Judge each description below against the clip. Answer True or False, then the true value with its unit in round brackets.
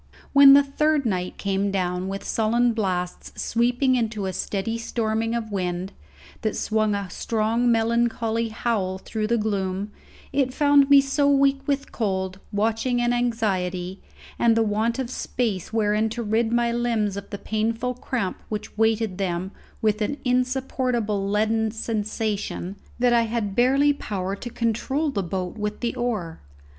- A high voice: True (225 Hz)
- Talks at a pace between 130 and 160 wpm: True (155 wpm)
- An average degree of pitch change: True (3.2 semitones)